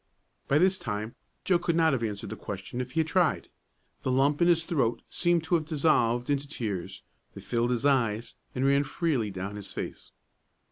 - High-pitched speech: No, low, 135 Hz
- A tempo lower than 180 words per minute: No, average, 195 wpm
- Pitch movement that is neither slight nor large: No, wide, 5.8 semitones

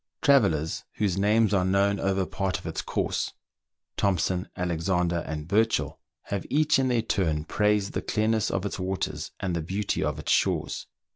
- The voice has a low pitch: Yes, very low, 95 Hz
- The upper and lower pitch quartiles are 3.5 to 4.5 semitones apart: No, average, 2.9 semitones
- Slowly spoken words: No, average, 165 wpm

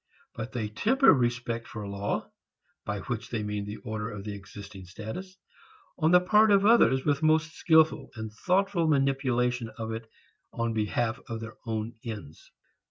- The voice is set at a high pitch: No, low, 120 Hz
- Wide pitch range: Yes, wide, 6.4 semitones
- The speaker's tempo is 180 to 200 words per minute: No, average, 165 wpm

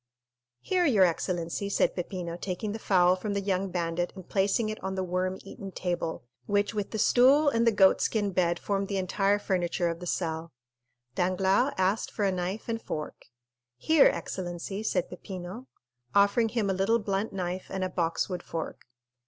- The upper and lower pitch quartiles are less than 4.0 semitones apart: Yes, narrow, 2.5 semitones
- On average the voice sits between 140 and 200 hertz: Yes, high, 190 Hz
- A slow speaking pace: No, average, 175 wpm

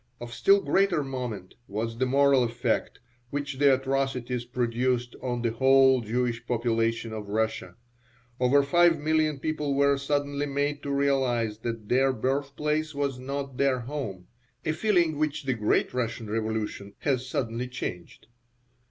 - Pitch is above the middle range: No, low, 130 Hz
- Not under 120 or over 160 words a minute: Yes, average, 145 wpm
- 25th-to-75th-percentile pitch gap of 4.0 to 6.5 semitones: No, average, 3.4 semitones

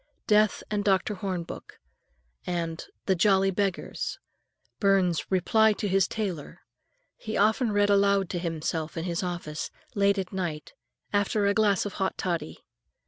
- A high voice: Yes, high, 195 Hz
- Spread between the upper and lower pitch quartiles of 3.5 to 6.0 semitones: No, average, 2.8 semitones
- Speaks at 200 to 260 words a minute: No, average, 140 wpm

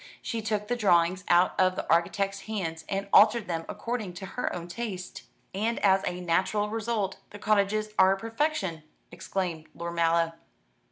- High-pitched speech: Yes, high, 195 Hz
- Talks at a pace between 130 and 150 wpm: No, average, 160 wpm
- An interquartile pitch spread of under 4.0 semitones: Yes, average, 3.6 semitones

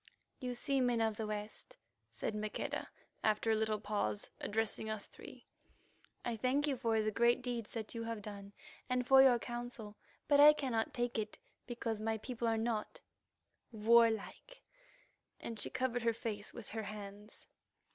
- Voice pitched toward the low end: No, high, 225 Hz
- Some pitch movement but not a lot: No, narrow, 2.3 semitones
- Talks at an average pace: Yes, average, 160 wpm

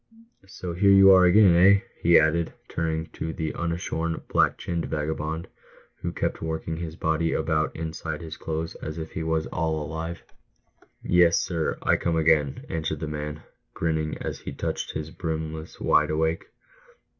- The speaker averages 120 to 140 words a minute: No, average, 170 wpm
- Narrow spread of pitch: Yes, narrow, 1.3 semitones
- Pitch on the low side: Yes, very low, 80 Hz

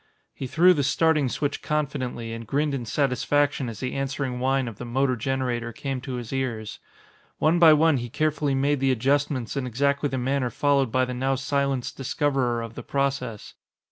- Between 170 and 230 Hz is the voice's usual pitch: No, low, 135 Hz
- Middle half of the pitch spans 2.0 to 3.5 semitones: Yes, narrow, 2.5 semitones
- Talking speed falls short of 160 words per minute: No, average, 185 wpm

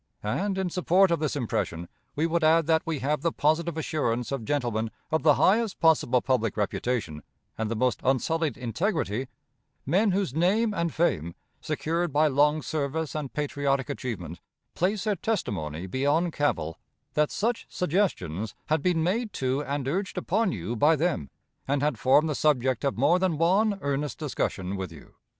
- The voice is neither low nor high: Yes, medium, 150 Hz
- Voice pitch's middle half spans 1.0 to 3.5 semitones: No, average, 5.3 semitones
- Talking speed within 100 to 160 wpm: No, average, 170 wpm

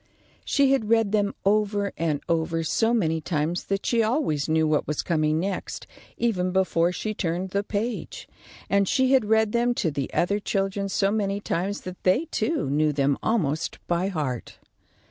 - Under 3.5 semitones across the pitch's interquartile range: No, average, 4.8 semitones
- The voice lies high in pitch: Yes, high, 195 Hz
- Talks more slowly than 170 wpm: No, average, 175 wpm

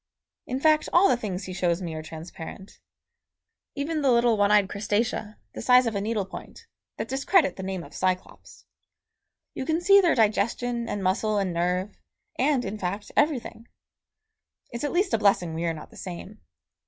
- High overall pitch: Yes, high, 210 Hz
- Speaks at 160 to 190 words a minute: Yes, average, 180 wpm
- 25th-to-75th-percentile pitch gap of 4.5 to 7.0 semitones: Yes, wide, 5.4 semitones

